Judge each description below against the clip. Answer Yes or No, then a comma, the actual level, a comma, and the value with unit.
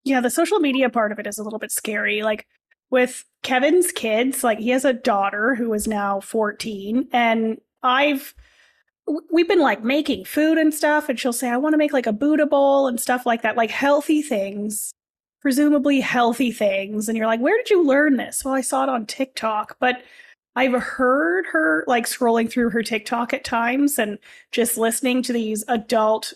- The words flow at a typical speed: Yes, average, 195 wpm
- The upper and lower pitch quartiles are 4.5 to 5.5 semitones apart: No, average, 3.8 semitones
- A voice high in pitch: Yes, very high, 250 Hz